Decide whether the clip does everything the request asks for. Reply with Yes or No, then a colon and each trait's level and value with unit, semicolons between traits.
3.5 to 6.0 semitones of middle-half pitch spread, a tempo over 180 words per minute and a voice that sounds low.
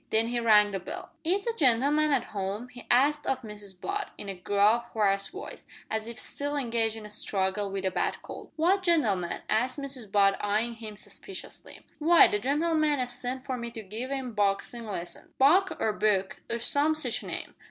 No: wide, 5.5 semitones; average, 195 wpm; high, 235 Hz